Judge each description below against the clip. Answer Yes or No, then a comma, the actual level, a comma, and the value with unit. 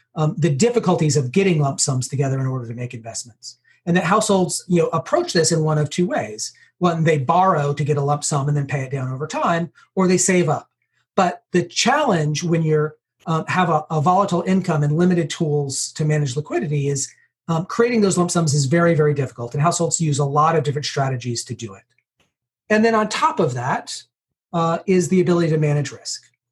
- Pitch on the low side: No, medium, 155 Hz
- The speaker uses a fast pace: Yes, fast, 215 wpm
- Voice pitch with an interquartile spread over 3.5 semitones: Yes, average, 4.0 semitones